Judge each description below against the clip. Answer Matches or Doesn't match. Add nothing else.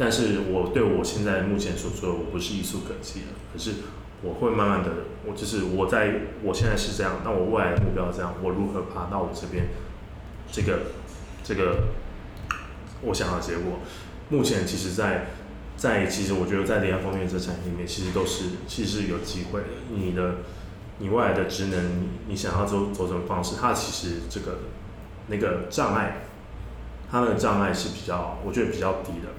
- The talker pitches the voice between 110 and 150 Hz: Doesn't match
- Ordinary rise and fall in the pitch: Doesn't match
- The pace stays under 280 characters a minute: Doesn't match